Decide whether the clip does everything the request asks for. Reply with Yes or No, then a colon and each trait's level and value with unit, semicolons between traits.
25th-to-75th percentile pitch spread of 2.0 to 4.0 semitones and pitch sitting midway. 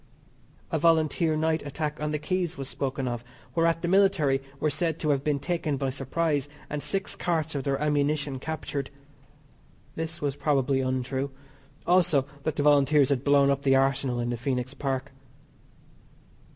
Yes: average, 2.8 semitones; medium, 145 Hz